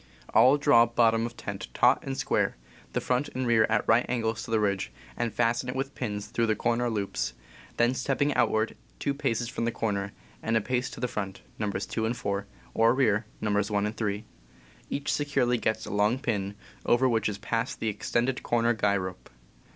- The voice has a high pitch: No, low, 115 Hz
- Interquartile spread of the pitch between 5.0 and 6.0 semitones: No, average, 2.9 semitones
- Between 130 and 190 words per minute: No, average, 200 wpm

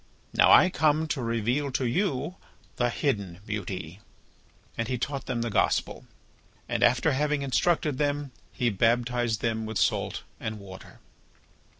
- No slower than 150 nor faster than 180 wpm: No, average, 140 wpm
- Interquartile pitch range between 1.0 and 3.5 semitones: No, average, 4.6 semitones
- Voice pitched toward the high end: No, low, 120 Hz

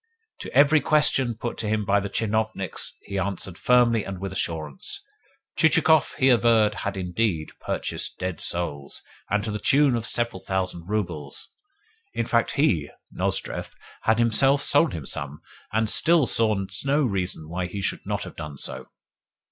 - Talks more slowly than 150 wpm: No, average, 160 wpm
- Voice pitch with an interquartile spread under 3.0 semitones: No, average, 4.7 semitones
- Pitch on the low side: Yes, low, 105 Hz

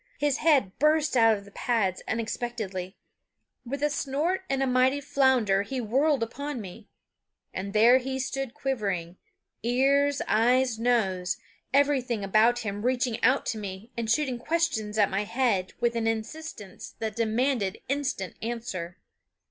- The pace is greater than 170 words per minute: No, average, 145 wpm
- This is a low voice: No, high, 240 Hz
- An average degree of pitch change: Yes, average, 4.4 semitones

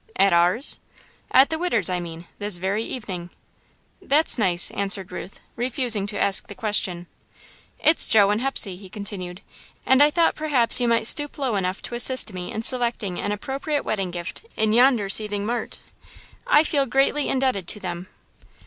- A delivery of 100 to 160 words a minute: No, average, 170 wpm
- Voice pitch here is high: Yes, high, 215 Hz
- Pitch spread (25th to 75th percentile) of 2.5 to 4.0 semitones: No, wide, 5.5 semitones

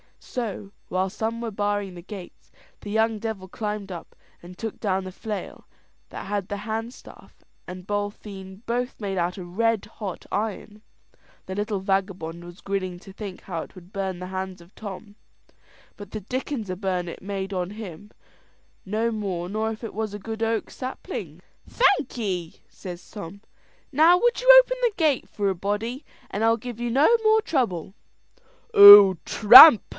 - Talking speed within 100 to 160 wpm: No, average, 170 wpm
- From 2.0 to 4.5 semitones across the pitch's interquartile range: Yes, average, 3.1 semitones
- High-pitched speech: Yes, high, 205 Hz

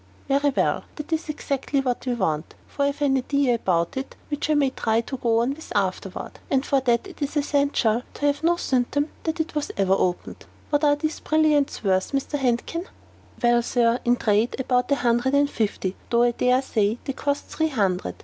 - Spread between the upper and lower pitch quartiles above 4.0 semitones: No, average, 3.7 semitones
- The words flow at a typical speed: No, fast, 215 wpm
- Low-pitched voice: No, very high, 265 Hz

